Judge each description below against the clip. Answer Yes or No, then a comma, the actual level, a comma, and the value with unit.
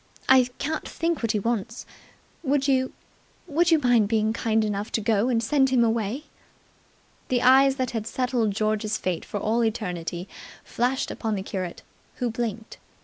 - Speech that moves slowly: No, average, 165 wpm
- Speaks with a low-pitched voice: No, high, 230 Hz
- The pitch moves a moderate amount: Yes, average, 3.3 semitones